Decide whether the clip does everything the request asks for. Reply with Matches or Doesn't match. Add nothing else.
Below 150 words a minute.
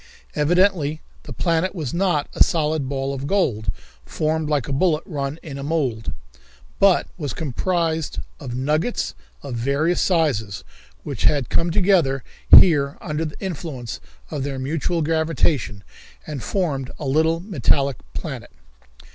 Matches